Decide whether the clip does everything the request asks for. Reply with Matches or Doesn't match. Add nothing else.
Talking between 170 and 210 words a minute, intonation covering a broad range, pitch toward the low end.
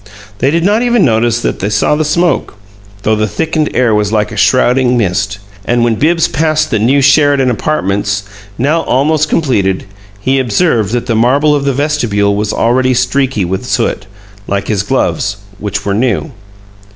Matches